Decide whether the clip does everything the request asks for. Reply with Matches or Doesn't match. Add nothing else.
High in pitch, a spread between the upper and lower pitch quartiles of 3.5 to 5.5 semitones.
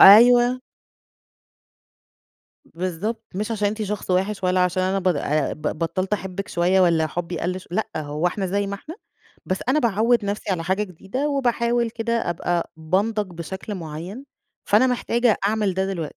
Matches